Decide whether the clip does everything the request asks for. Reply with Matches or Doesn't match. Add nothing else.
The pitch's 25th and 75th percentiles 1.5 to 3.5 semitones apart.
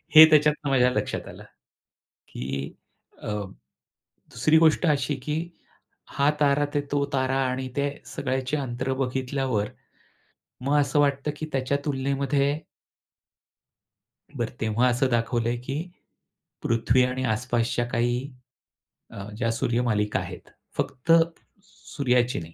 Matches